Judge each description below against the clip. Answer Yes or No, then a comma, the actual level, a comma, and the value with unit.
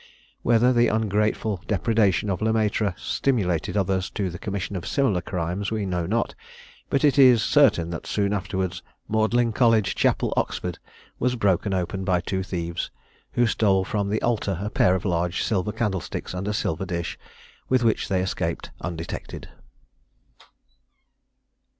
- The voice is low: Yes, low, 100 Hz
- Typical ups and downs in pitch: Yes, average, 3.4 semitones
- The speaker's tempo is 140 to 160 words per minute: Yes, average, 150 wpm